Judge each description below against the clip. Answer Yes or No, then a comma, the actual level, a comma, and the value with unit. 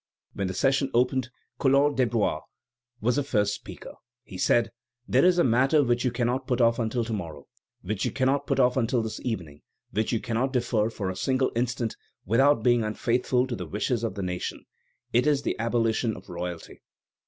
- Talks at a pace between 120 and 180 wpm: No, average, 190 wpm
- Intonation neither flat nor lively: Yes, average, 3.3 semitones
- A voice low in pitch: Yes, low, 120 Hz